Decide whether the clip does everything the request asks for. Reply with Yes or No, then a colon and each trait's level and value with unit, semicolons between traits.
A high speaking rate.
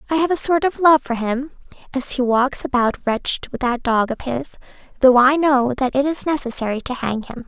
Yes: fast, 225 wpm